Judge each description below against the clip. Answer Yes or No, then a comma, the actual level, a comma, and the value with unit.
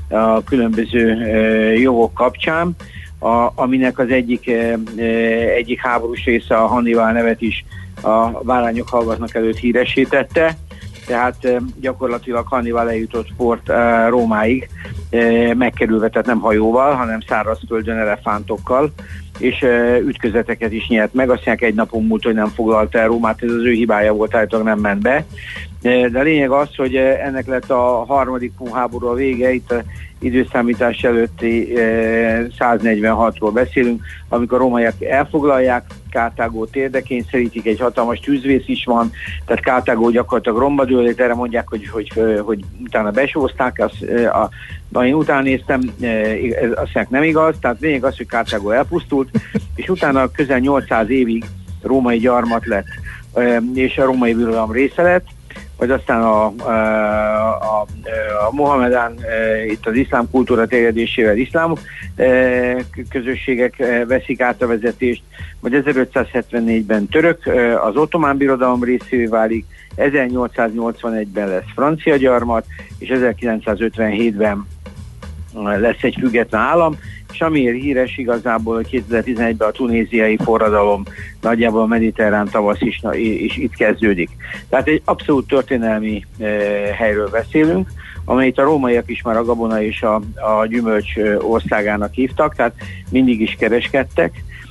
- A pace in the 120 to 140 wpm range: Yes, average, 135 wpm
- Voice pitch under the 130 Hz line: Yes, low, 115 Hz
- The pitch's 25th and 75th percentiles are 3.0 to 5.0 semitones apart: No, narrow, 2.5 semitones